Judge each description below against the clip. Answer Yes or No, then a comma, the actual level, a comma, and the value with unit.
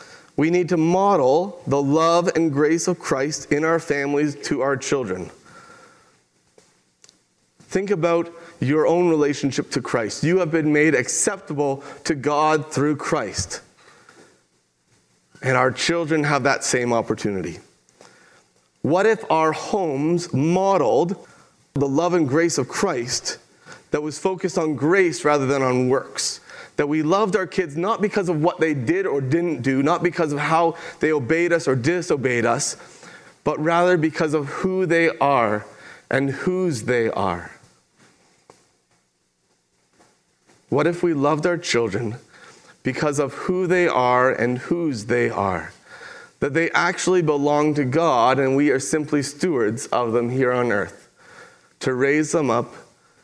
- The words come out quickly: No, average, 145 wpm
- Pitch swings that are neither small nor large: Yes, average, 4.0 semitones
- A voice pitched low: No, medium, 155 Hz